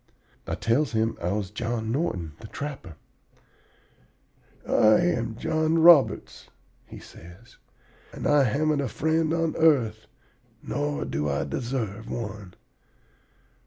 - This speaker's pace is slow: Yes, slow, 125 wpm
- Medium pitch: No, low, 120 Hz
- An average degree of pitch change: No, wide, 6.2 semitones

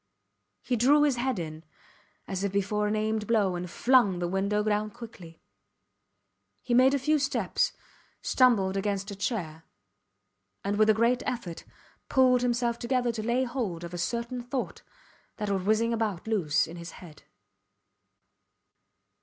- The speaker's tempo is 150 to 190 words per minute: Yes, average, 155 wpm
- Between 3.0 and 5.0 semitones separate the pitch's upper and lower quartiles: Yes, average, 4.2 semitones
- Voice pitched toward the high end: Yes, high, 215 Hz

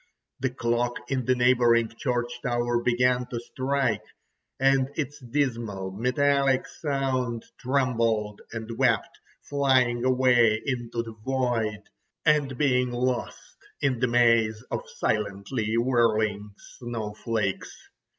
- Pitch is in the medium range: No, low, 120 Hz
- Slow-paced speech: Yes, slow, 110 wpm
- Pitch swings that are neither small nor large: No, narrow, 2.2 semitones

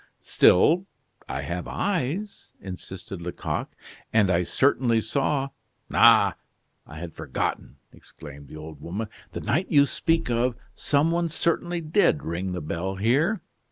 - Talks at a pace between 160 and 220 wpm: No, average, 140 wpm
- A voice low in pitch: Yes, low, 120 Hz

